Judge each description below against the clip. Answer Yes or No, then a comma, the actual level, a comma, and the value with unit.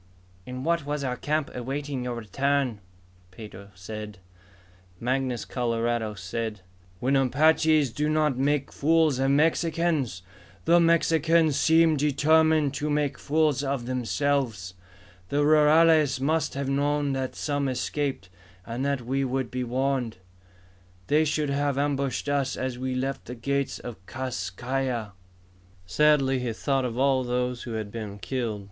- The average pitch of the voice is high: No, low, 135 Hz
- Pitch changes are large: No, average, 3.3 semitones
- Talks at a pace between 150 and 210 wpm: No, average, 140 wpm